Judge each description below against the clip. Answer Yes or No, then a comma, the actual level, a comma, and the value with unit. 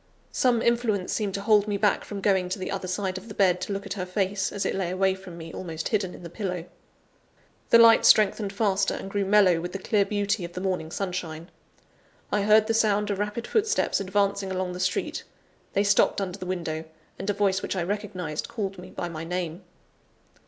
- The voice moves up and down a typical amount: No, narrow, 2.1 semitones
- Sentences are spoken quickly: Yes, fast, 215 wpm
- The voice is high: Yes, high, 195 Hz